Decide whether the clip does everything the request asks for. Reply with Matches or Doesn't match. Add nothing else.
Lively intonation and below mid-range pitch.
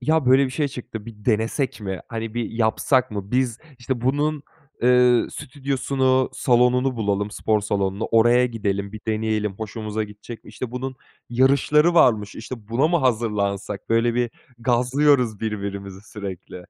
Doesn't match